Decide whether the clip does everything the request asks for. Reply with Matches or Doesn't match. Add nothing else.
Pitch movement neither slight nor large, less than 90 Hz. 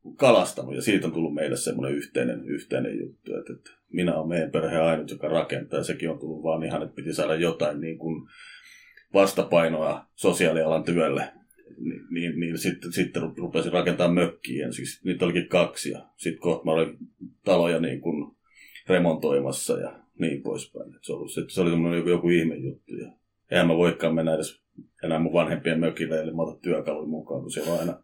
Doesn't match